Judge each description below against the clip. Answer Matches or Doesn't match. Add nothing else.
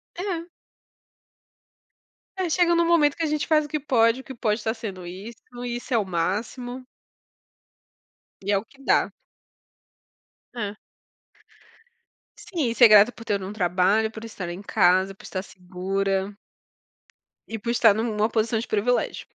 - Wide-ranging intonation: Doesn't match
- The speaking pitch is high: Matches